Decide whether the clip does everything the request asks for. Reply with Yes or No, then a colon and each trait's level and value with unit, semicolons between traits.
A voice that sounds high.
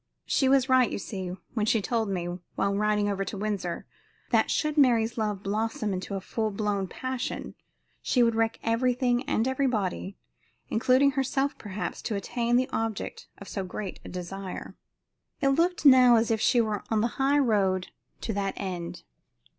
Yes: high, 220 Hz